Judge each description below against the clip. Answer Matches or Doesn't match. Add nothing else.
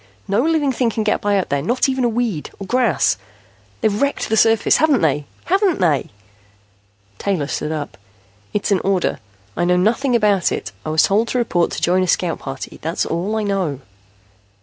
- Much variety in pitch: Matches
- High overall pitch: Matches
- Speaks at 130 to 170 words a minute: Doesn't match